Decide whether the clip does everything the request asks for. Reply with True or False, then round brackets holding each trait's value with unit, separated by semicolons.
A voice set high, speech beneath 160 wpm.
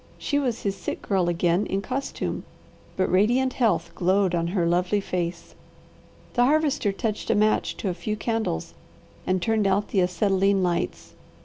False (195 Hz; 165 wpm)